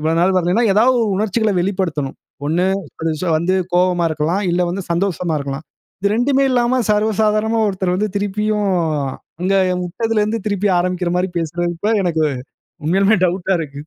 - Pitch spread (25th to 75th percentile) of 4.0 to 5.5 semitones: No, average, 3.6 semitones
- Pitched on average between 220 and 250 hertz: No, high, 190 Hz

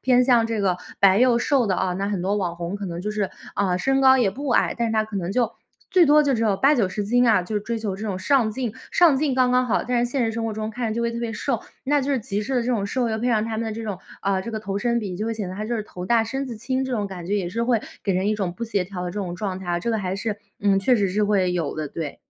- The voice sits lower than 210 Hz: No, high, 215 Hz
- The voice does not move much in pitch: No, average, 3.8 semitones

